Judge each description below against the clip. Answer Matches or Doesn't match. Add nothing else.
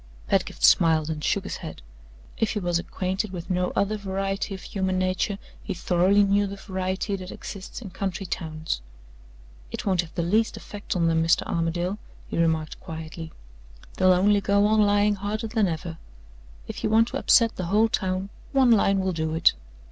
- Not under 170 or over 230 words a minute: Matches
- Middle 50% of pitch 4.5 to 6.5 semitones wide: Doesn't match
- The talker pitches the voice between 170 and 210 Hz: Matches